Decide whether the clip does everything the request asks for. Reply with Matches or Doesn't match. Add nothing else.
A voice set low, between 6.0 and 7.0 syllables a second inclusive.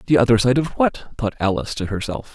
Matches